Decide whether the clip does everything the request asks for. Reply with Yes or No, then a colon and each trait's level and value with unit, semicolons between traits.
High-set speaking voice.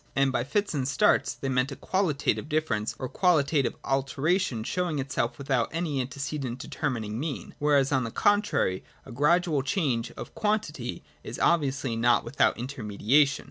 No: medium, 140 Hz